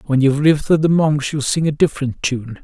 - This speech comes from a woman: No, male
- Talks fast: Yes, fast, 250 wpm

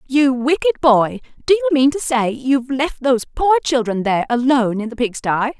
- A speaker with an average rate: Yes, average, 195 wpm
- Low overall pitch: No, very high, 265 Hz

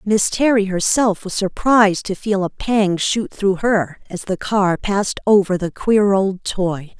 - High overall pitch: Yes, high, 200 Hz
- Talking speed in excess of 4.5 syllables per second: No, 4.0 syllables/s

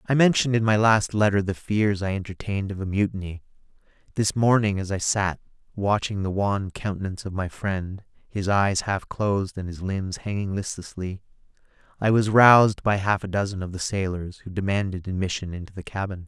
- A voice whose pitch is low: Yes, low, 100 Hz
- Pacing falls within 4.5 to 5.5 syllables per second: Yes, 5.4 syllables/s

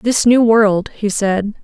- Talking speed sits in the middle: Yes, average, 185 wpm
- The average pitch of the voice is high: Yes, high, 215 Hz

